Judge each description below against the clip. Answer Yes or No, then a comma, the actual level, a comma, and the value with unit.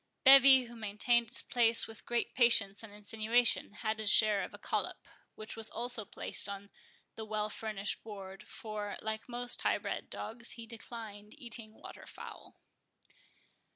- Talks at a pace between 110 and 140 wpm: No, average, 155 wpm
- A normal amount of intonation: No, narrow, 2.1 semitones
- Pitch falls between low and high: No, high, 220 Hz